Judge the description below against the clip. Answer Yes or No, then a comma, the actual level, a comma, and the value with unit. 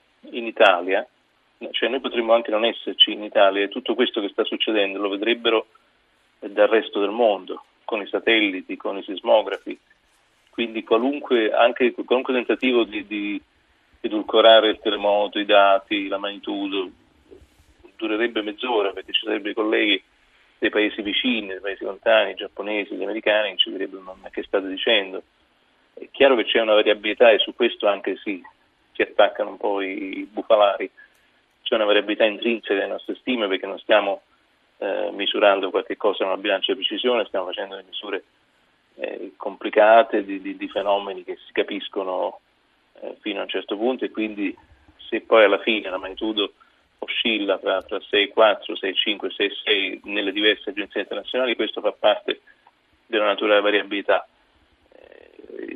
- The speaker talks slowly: No, average, 160 wpm